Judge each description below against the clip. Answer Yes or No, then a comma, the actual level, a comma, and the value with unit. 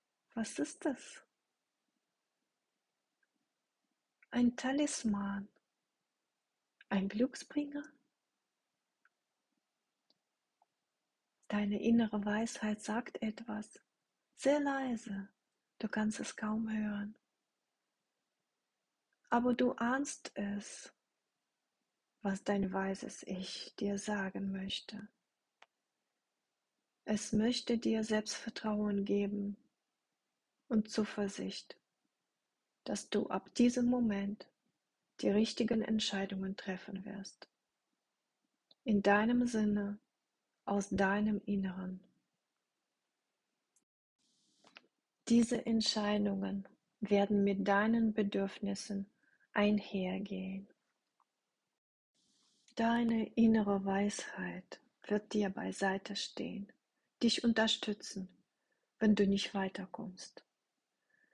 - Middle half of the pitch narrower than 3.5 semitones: Yes, average, 2.7 semitones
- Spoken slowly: Yes, slow, 70 wpm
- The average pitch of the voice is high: Yes, high, 210 Hz